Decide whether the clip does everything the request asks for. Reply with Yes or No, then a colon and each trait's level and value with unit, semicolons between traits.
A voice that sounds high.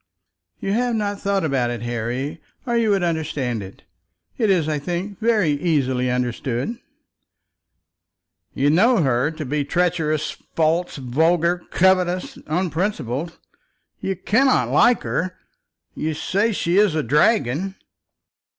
No: medium, 165 Hz